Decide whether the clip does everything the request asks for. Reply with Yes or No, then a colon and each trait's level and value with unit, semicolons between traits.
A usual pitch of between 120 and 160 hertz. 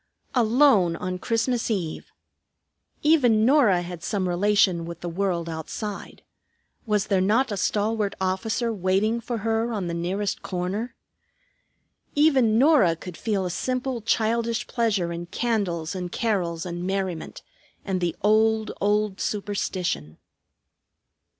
No: high, 205 Hz